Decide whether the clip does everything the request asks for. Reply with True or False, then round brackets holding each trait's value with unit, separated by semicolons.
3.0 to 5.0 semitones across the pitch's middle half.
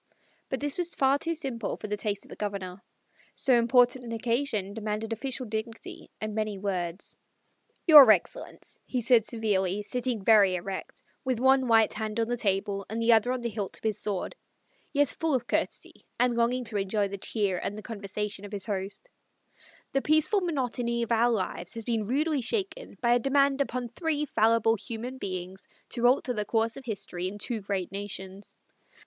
True (3.8 semitones)